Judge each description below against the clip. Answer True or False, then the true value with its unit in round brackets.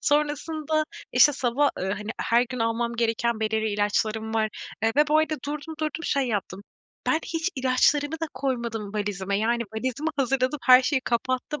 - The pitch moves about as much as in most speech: True (4.9 semitones)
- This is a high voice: True (255 Hz)